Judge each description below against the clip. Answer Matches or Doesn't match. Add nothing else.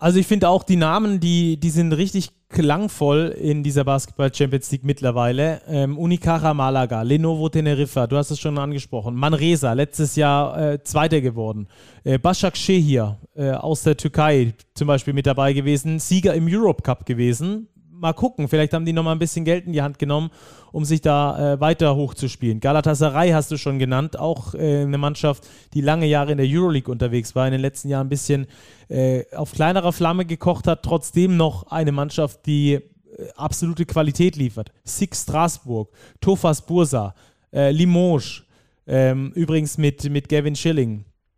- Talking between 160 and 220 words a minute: Matches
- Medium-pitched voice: Matches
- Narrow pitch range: Doesn't match